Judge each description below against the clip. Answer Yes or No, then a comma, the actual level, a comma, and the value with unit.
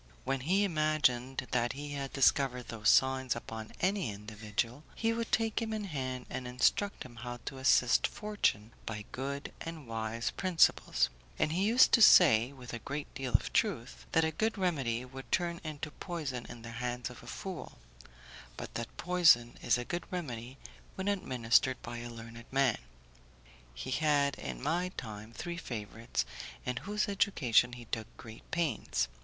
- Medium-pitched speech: No, low, 130 Hz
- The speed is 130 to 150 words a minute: No, average, 170 wpm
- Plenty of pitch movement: Yes, wide, 6.0 semitones